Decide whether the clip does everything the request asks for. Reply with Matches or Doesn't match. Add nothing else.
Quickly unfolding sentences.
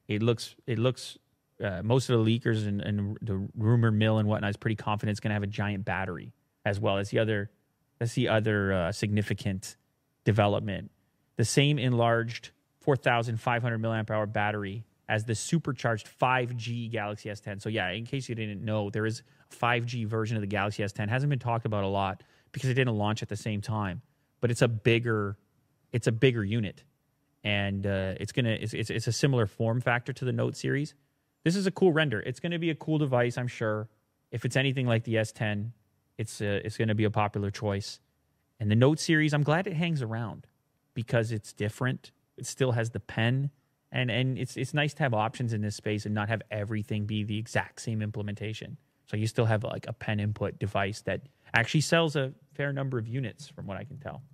Matches